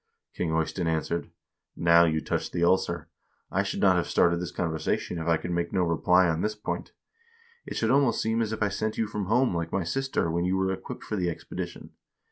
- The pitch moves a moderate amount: Yes, average, 3.8 semitones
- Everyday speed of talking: No, fast, 225 wpm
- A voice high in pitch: No, very low, 90 Hz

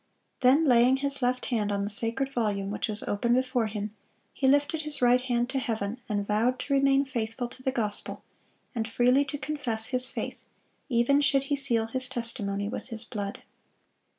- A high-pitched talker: Yes, high, 245 Hz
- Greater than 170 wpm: Yes, average, 185 wpm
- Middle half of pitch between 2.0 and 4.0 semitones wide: Yes, average, 3.6 semitones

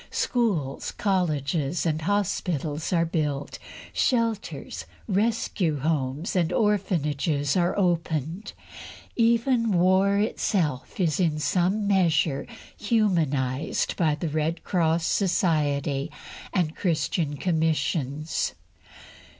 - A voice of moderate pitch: Yes, medium, 165 Hz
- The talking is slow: Yes, slow, 90 wpm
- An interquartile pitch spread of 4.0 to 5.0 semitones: Yes, average, 4.5 semitones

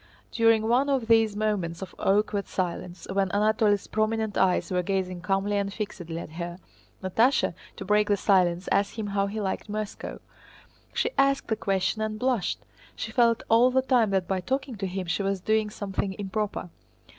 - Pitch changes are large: No, narrow, 2.5 semitones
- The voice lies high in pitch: Yes, high, 205 Hz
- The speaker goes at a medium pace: Yes, average, 180 wpm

